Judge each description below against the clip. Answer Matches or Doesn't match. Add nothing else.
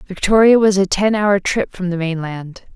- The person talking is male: Doesn't match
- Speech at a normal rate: Matches